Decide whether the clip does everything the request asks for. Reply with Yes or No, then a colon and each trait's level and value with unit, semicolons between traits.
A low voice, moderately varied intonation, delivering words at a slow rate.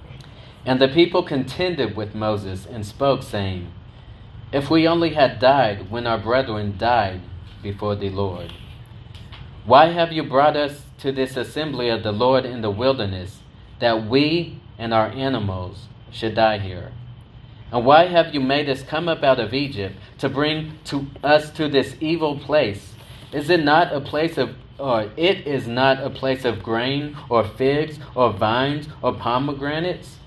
No: low, 125 Hz; average, 4.7 semitones; average, 165 wpm